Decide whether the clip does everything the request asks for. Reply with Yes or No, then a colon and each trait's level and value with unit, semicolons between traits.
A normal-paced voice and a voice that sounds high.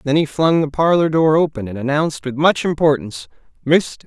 No: average, 190 wpm; medium, 150 Hz